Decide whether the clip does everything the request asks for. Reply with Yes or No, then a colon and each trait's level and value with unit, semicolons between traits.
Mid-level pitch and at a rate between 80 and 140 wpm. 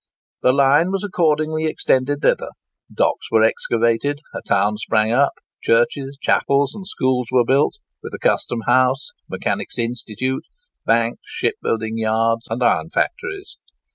No: low, 130 Hz; slow, 135 wpm